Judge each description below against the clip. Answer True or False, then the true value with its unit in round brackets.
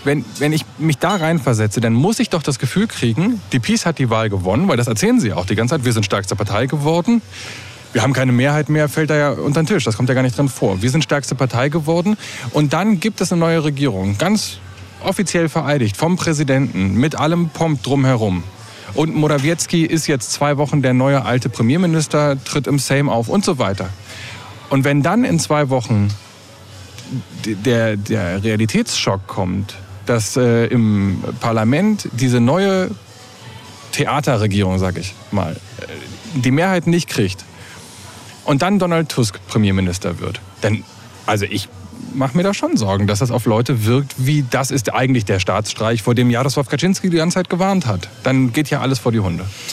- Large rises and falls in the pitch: True (5.9 semitones)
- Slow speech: False (185 wpm)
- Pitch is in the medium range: False (130 Hz)